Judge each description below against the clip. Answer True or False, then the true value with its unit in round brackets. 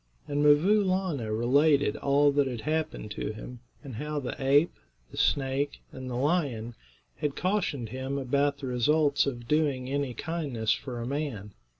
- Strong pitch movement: False (3.1 semitones)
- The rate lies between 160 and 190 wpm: True (165 wpm)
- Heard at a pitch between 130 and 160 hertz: True (140 Hz)